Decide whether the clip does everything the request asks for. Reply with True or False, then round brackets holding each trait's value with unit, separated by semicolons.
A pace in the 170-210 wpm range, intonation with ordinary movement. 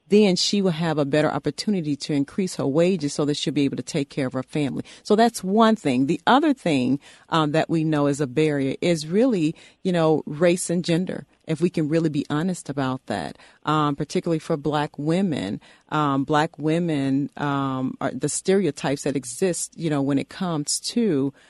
True (200 wpm; 3.7 semitones)